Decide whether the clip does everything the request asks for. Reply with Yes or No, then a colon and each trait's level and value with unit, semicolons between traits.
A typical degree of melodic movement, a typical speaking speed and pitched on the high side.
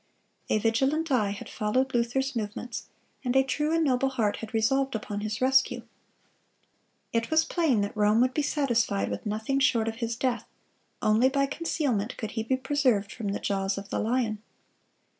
Yes: average, 3.9 semitones; average, 180 wpm; high, 235 Hz